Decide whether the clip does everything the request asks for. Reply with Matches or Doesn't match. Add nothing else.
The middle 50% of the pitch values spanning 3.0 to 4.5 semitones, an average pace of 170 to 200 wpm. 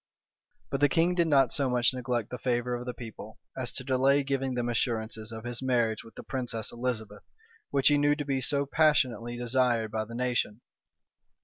Doesn't match